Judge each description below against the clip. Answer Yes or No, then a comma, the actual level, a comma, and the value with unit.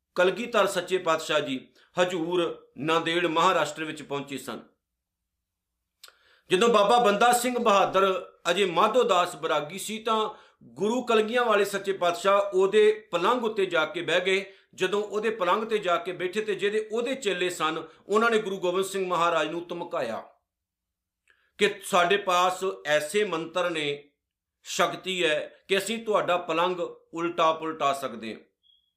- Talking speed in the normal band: Yes, average, 140 wpm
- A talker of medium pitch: Yes, medium, 180 Hz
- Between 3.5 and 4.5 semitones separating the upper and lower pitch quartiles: Yes, average, 4.2 semitones